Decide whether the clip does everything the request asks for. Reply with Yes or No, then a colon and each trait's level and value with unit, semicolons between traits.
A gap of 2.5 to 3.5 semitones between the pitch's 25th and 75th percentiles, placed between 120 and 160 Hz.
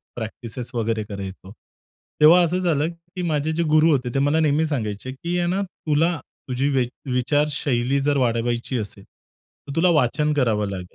No: average, 5.1 semitones; medium, 140 Hz